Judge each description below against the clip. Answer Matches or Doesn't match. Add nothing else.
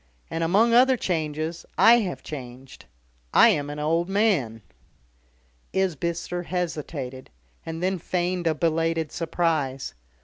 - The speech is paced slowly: Matches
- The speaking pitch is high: Doesn't match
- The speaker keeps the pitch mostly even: Doesn't match